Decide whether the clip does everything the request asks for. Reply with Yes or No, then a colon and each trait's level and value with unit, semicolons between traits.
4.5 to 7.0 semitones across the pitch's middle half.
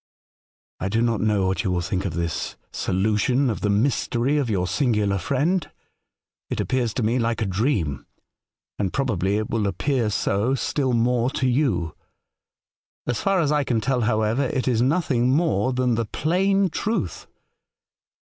Yes: average, 4.8 semitones